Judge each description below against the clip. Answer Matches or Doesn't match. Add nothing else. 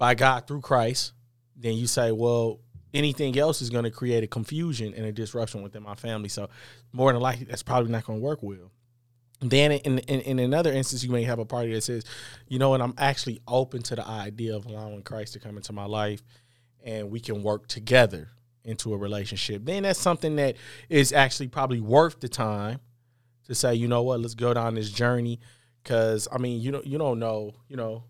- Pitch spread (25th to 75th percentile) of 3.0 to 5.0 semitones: Doesn't match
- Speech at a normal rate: Doesn't match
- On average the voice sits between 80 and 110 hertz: Doesn't match